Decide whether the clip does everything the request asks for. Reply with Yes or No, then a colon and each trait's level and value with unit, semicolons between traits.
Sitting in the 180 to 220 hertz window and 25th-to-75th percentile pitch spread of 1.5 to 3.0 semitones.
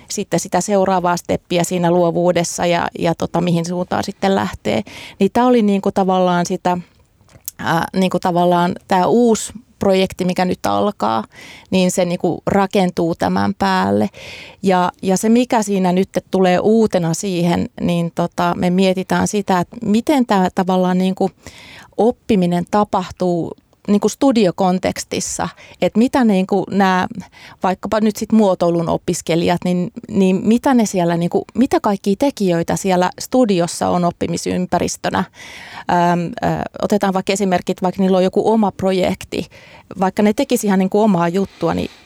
Yes: medium, 185 Hz; narrow, 2.5 semitones